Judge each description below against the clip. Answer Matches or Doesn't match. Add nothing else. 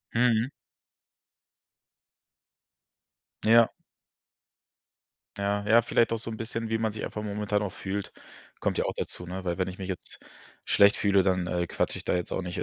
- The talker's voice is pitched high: Doesn't match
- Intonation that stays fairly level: Doesn't match